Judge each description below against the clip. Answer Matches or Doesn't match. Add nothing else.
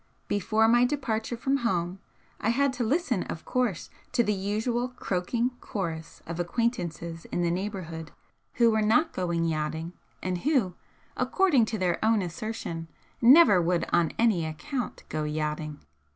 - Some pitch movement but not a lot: Doesn't match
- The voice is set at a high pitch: Matches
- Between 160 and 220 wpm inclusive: Doesn't match